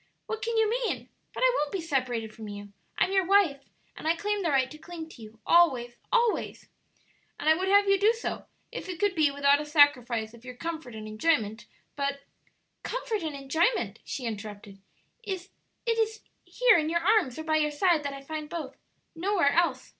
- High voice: Yes, very high, 315 Hz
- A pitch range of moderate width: No, wide, 7.0 semitones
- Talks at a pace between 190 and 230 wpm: Yes, average, 200 wpm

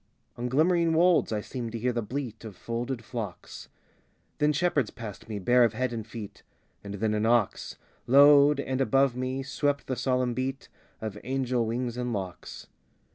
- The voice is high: No, low, 125 Hz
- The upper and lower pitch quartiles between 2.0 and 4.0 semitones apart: Yes, average, 3.3 semitones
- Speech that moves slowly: No, average, 175 wpm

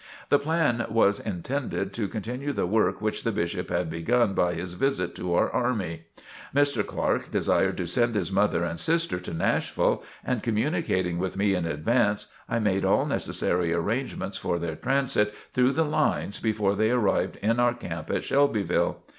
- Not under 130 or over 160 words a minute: No, average, 170 wpm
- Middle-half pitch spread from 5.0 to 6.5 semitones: Yes, wide, 5.5 semitones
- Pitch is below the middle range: Yes, low, 105 Hz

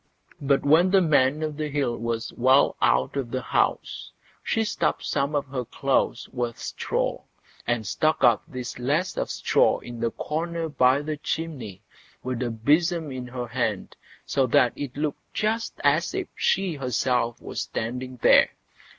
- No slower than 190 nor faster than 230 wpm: No, average, 165 wpm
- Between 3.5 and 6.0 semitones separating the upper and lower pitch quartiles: Yes, average, 4.1 semitones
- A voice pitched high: No, low, 135 Hz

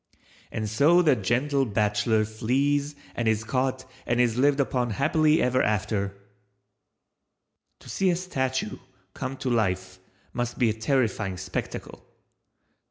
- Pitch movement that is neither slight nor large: Yes, average, 4.3 semitones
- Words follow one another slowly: Yes, slow, 130 wpm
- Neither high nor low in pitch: No, low, 125 Hz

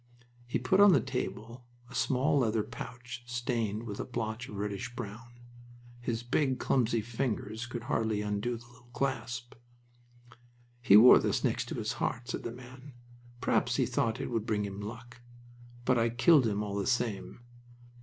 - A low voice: Yes, low, 120 Hz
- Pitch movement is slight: Yes, narrow, 2.3 semitones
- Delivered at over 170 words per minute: No, average, 165 wpm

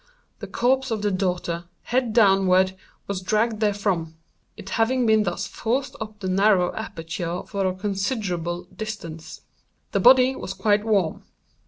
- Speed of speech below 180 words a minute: Yes, average, 145 wpm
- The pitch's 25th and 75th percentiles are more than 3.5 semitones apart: No, average, 3.2 semitones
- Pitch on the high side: Yes, high, 200 Hz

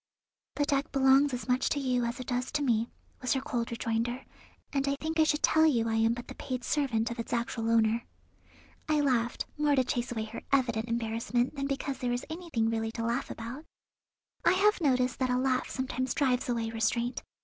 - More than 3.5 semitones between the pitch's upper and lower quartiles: No, average, 3.0 semitones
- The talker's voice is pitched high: Yes, very high, 250 Hz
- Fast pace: Yes, fast, 210 wpm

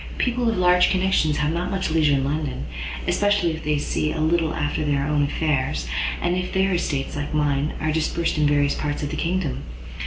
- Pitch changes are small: No, average, 3.4 semitones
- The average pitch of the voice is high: No, medium, 155 Hz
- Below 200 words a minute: No, fast, 205 wpm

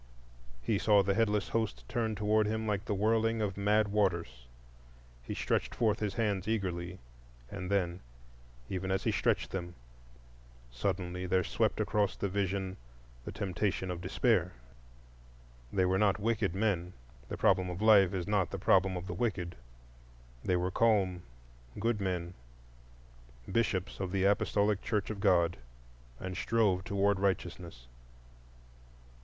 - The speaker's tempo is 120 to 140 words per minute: Yes, slow, 135 wpm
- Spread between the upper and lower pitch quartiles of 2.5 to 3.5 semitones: Yes, average, 2.9 semitones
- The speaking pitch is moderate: No, very low, 95 Hz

